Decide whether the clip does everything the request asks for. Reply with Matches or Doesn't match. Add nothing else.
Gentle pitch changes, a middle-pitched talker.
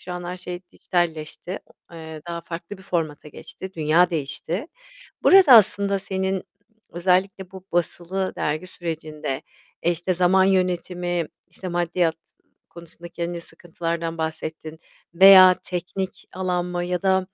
Matches